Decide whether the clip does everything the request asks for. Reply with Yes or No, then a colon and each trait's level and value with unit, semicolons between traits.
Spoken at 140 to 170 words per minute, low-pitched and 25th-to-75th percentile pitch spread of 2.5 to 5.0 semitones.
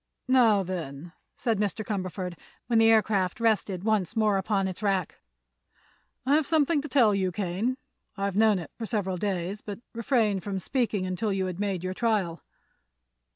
No: average, 160 wpm; high, 200 Hz; average, 3.3 semitones